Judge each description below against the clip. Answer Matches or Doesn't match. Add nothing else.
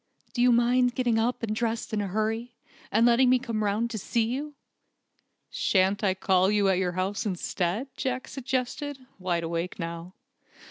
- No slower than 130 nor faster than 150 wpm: Doesn't match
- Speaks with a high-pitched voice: Matches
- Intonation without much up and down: Doesn't match